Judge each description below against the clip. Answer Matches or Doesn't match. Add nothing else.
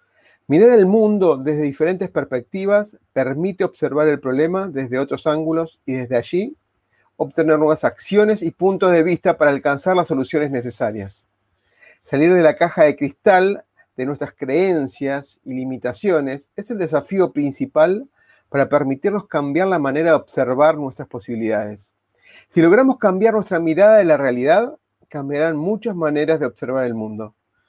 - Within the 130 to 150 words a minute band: Matches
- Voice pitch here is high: Doesn't match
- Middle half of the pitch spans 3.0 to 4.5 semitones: Doesn't match